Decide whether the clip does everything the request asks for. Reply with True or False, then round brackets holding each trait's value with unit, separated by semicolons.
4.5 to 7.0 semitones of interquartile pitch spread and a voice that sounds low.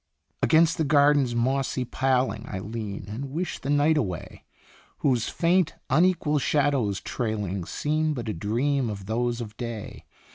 True (5.1 semitones; 130 Hz)